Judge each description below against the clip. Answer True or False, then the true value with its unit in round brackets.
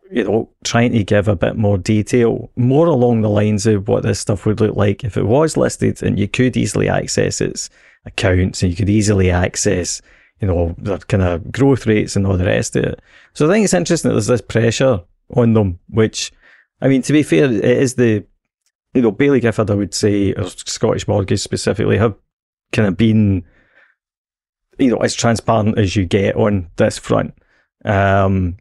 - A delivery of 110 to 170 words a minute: False (200 wpm)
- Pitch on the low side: True (110 Hz)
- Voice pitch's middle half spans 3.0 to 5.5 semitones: True (3.6 semitones)